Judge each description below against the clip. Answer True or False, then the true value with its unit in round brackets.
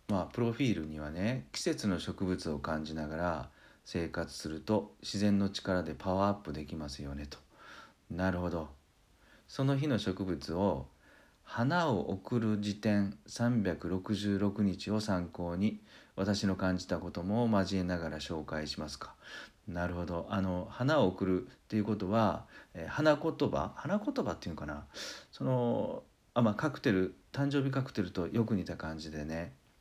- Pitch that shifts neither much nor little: True (4.3 semitones)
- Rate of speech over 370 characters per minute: False (285 characters per minute)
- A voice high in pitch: False (95 Hz)